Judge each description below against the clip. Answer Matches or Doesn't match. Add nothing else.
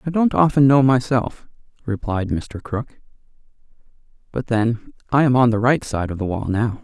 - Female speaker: Doesn't match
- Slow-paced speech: Doesn't match